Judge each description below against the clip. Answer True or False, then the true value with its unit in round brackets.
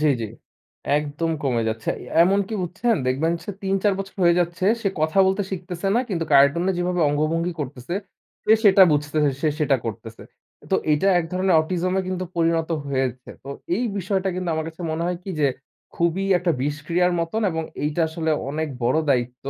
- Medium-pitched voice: True (165 Hz)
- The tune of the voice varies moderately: True (3.8 semitones)